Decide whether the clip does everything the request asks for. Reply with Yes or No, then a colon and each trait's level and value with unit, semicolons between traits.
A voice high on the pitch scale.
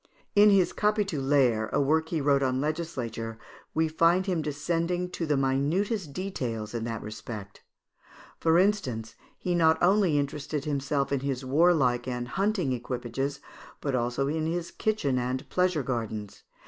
No: medium, 145 Hz